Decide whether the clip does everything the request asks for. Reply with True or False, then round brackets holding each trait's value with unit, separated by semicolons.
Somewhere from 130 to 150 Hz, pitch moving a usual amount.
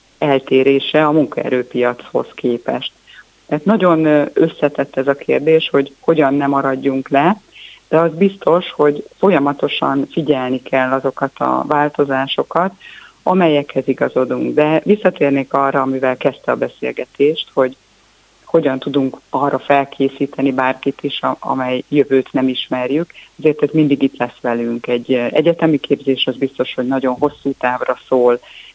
False (140 Hz; 2.3 semitones)